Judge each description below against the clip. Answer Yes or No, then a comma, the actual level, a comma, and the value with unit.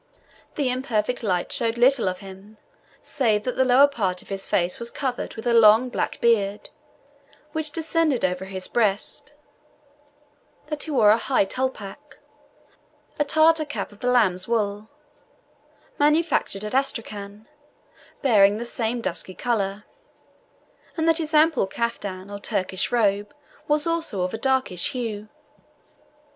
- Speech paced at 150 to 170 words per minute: No, average, 140 wpm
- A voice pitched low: No, high, 230 Hz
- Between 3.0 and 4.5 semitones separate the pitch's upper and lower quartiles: No, average, 5.0 semitones